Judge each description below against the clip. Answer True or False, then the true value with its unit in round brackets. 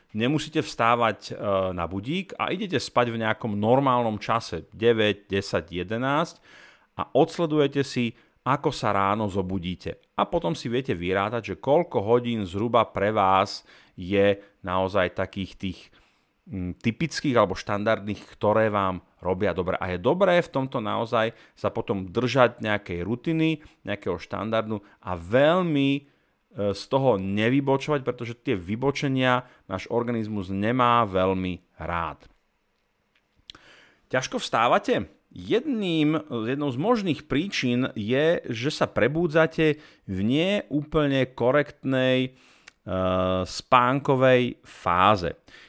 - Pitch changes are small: False (5.6 semitones)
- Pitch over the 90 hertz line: True (115 Hz)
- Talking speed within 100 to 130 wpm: True (115 wpm)